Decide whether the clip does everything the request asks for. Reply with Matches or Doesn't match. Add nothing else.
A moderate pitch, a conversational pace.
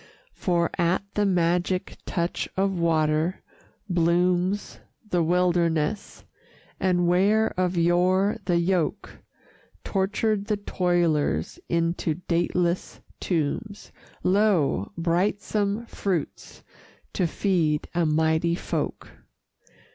Doesn't match